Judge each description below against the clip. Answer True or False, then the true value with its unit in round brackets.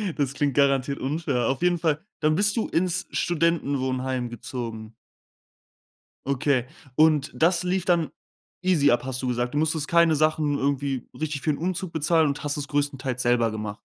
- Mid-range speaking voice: True (145 Hz)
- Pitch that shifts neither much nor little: True (3.8 semitones)